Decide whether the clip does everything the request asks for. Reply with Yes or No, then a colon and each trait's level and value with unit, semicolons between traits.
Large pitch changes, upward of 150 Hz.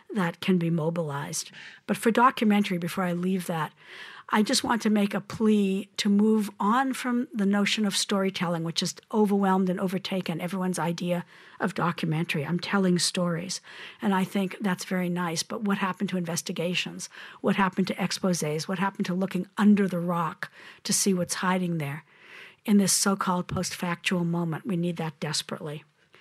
No: narrow, 2.5 semitones; medium, 185 Hz